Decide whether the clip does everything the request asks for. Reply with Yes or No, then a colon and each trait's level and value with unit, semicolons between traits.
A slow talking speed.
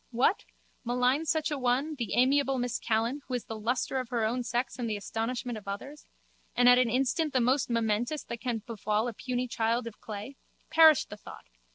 No: fast, 205 wpm